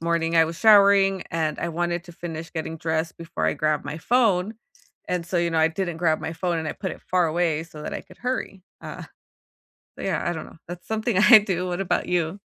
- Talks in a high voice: No, medium, 170 Hz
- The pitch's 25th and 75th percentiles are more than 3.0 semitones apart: No, narrow, 2.6 semitones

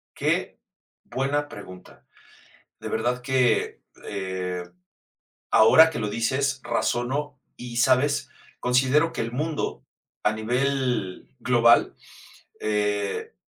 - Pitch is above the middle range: No, low, 125 Hz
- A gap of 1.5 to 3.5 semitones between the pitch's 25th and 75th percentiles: No, average, 4.2 semitones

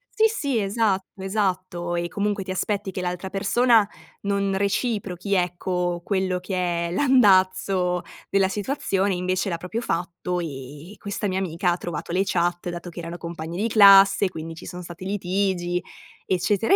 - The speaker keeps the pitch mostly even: Yes, narrow, 2.3 semitones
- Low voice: No, medium, 185 Hz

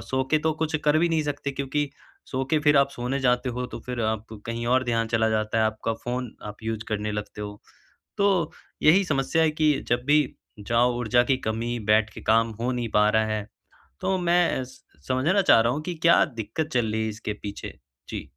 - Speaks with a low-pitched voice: Yes, low, 125 Hz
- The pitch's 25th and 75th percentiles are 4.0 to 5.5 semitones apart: Yes, average, 4.8 semitones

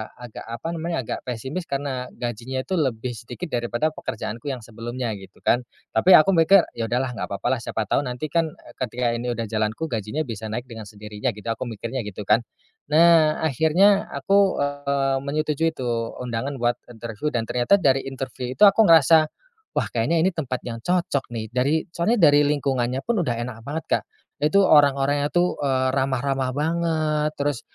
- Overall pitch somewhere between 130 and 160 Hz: Yes, low, 135 Hz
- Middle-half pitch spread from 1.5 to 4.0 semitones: No, average, 4.8 semitones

